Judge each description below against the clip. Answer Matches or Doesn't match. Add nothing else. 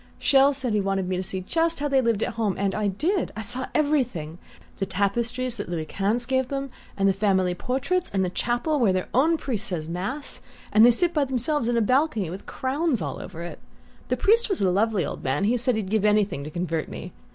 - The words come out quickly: Matches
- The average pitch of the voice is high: Matches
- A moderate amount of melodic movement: Doesn't match